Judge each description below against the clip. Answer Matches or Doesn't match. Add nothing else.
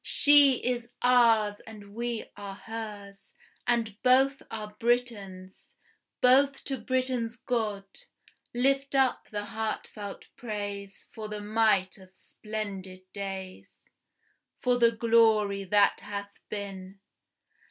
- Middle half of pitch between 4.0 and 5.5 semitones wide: Doesn't match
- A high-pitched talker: Matches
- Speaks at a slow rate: Matches